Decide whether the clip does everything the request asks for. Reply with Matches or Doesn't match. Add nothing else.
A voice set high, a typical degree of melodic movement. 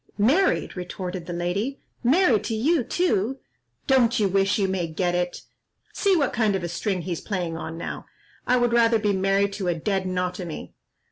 Matches